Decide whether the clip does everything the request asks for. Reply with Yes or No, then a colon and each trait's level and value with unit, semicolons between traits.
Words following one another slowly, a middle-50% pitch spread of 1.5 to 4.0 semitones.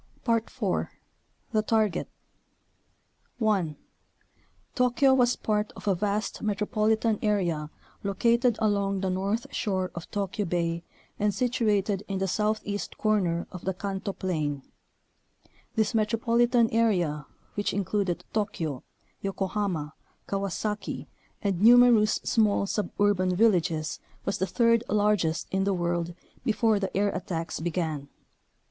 Yes: slow, 115 wpm; average, 3.2 semitones